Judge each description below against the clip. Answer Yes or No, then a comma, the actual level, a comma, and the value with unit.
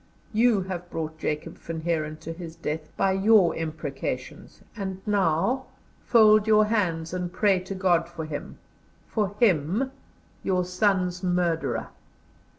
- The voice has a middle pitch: Yes, medium, 180 Hz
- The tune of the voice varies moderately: Yes, average, 3.8 semitones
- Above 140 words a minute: No, slow, 135 wpm